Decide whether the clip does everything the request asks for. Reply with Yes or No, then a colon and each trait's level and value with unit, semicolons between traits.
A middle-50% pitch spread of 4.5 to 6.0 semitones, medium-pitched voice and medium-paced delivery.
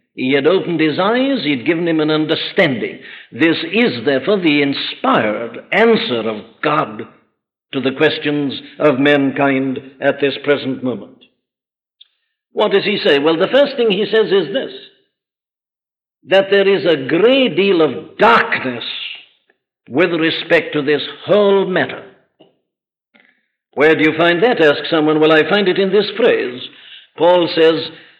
Yes: wide, 5.4 semitones; medium, 160 Hz; average, 145 wpm